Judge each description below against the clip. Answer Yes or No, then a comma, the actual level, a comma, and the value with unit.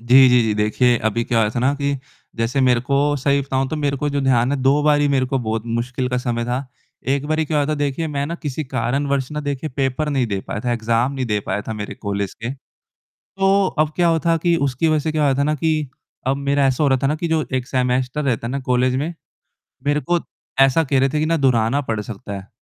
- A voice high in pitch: No, low, 135 Hz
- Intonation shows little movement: No, average, 3.2 semitones